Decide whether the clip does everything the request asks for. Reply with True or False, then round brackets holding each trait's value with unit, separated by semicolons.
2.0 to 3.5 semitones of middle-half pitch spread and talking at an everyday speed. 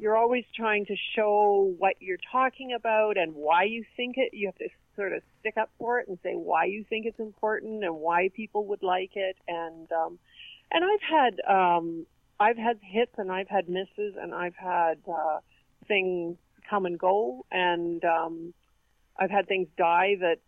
False (4.0 semitones; 190 wpm)